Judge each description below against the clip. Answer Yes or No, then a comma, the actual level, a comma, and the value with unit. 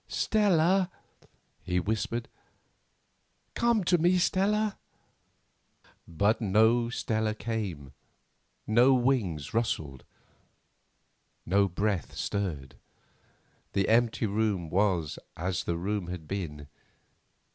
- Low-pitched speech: Yes, low, 105 Hz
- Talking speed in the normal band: No, slow, 90 wpm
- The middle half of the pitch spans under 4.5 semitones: No, wide, 5.4 semitones